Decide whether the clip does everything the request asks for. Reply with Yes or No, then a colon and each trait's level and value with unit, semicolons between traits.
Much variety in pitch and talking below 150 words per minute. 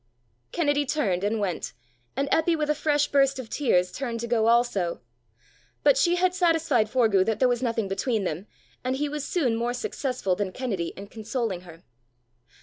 No: wide, 6.1 semitones; average, 180 wpm